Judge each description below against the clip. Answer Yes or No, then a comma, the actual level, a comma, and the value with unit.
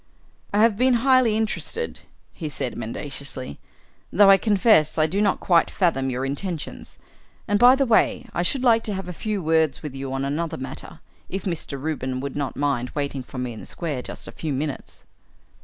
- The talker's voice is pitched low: No, medium, 160 Hz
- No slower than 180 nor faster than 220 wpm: Yes, average, 195 wpm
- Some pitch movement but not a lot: No, wide, 7.2 semitones